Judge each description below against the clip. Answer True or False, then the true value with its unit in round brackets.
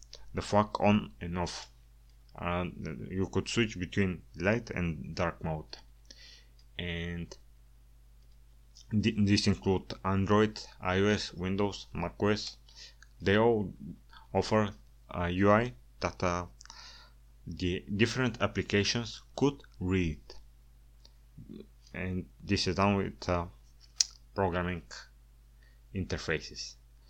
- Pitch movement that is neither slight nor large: False (9.0 semitones)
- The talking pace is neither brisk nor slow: False (95 wpm)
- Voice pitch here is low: True (90 Hz)